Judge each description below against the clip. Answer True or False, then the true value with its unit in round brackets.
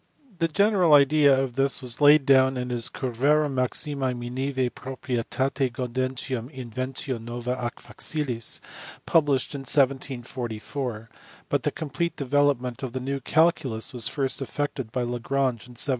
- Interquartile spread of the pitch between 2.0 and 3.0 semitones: True (2.4 semitones)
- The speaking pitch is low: True (130 Hz)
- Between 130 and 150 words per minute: True (140 wpm)